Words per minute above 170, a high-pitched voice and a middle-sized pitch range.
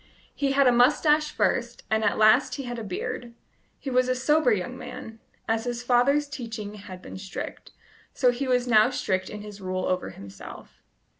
Yes: average, 190 wpm; high, 240 Hz; average, 3.5 semitones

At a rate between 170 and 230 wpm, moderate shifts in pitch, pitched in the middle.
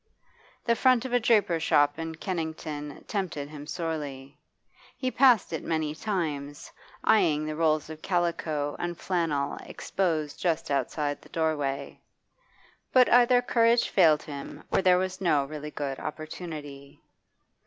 No: slow, 135 wpm; average, 4.3 semitones; medium, 160 Hz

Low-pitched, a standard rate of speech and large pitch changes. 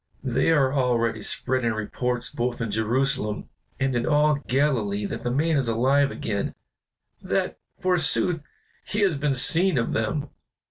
No: low, 130 Hz; average, 145 wpm; average, 4.1 semitones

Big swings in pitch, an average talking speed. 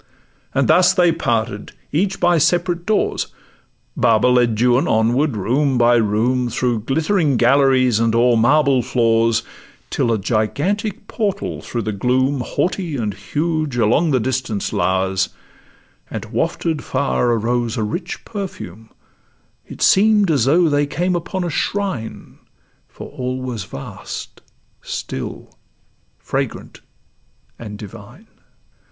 No: wide, 6.3 semitones; slow, 125 wpm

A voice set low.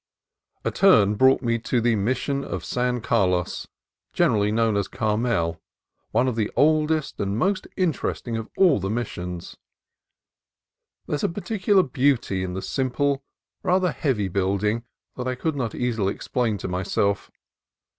Yes: low, 115 Hz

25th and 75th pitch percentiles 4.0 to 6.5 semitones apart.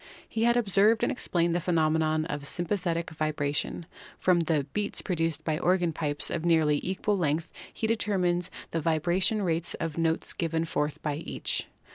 No: average, 2.8 semitones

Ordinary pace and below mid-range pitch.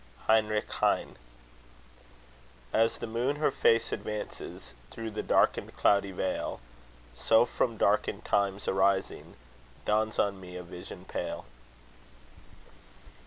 No: slow, 110 wpm; low, 105 Hz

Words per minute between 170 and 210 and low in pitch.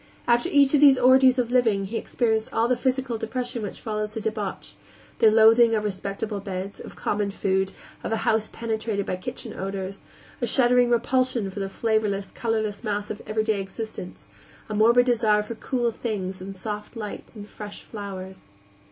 No: average, 175 wpm; high, 220 Hz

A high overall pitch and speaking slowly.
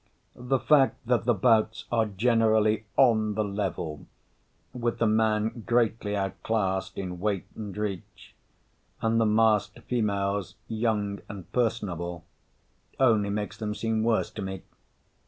No: low, 110 Hz; slow, 130 wpm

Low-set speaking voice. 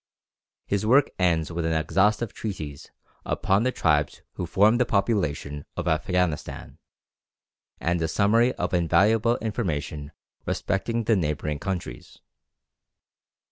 Yes: very low, 90 Hz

